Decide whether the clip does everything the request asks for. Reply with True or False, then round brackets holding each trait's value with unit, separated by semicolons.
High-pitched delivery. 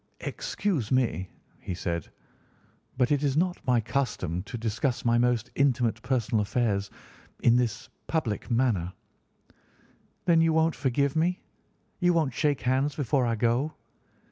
False (125 Hz)